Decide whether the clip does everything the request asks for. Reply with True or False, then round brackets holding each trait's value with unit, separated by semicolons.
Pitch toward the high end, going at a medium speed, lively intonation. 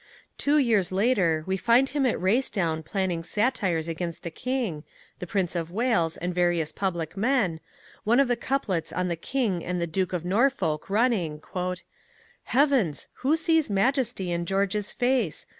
True (195 Hz; 160 wpm; 6.4 semitones)